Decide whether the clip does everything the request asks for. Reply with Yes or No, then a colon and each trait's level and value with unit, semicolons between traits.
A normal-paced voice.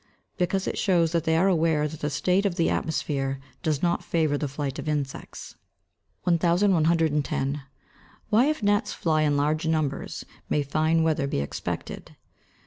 Yes: average, 160 wpm